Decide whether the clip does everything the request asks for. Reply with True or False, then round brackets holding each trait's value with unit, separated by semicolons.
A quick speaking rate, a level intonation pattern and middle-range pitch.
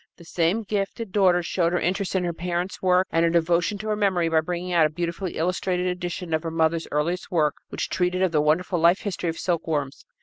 True (225 wpm; 1.9 semitones; 175 Hz)